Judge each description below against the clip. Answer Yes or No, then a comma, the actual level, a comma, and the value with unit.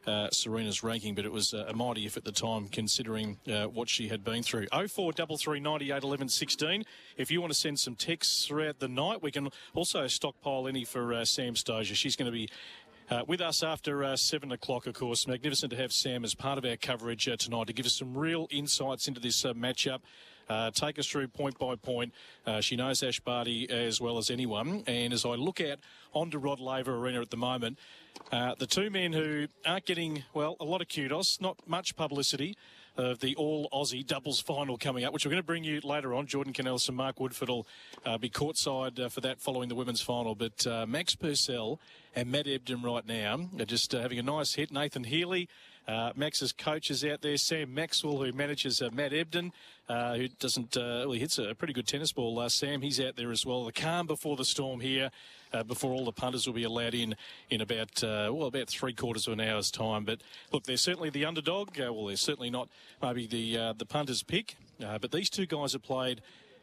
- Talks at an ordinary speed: No, fast, 230 wpm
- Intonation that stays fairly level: No, average, 3.8 semitones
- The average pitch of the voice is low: Yes, low, 130 Hz